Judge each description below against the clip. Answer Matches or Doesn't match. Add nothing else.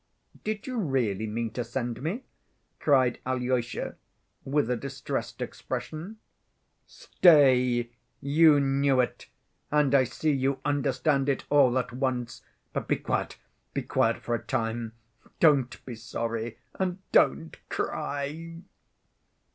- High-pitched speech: Doesn't match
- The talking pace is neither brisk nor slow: Doesn't match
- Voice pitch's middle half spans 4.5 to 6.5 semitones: Doesn't match